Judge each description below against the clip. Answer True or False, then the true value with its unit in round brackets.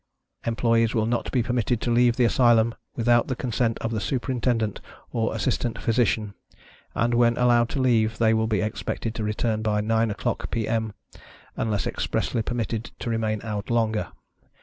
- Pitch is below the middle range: True (115 Hz)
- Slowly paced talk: False (165 wpm)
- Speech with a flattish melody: True (1.5 semitones)